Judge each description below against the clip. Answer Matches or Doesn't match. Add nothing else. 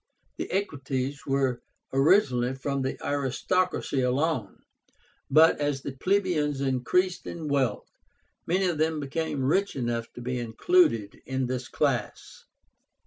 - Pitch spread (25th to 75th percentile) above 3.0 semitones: Matches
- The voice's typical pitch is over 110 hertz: Matches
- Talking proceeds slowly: Matches